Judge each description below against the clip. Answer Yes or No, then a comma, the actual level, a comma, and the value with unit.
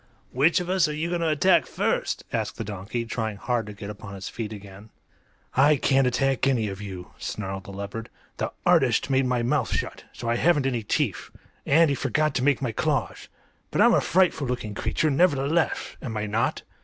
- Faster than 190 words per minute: Yes, fast, 205 wpm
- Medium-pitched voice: No, low, 125 Hz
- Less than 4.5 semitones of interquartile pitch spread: No, average, 5.3 semitones